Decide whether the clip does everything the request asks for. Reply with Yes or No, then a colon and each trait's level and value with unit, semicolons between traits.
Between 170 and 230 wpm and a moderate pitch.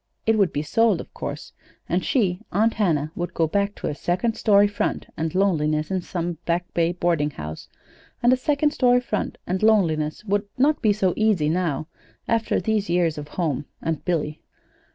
Yes: average, 180 wpm; medium, 180 Hz